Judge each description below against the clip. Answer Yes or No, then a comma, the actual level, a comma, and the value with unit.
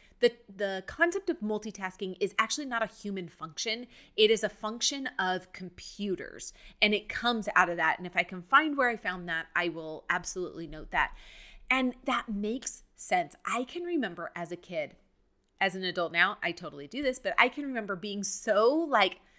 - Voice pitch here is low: No, high, 205 Hz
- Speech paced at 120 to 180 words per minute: No, average, 190 wpm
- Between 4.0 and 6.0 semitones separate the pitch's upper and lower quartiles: Yes, average, 5.0 semitones